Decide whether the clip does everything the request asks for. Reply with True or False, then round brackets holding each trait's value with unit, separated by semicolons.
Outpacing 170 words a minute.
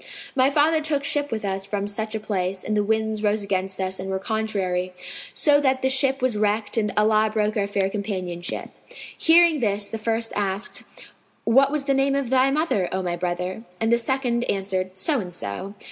True (200 wpm)